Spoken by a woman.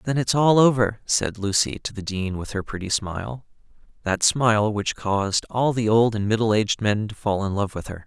No: male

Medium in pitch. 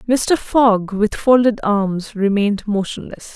No: high, 215 Hz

